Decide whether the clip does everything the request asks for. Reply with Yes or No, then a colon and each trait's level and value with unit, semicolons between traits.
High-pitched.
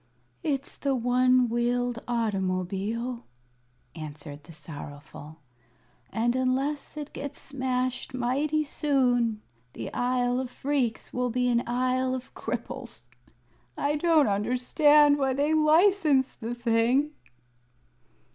Yes: very high, 250 Hz